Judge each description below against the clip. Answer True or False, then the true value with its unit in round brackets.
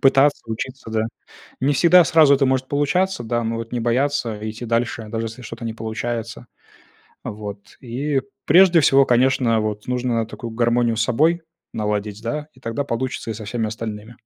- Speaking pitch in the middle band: False (120 Hz)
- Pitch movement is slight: False (3.2 semitones)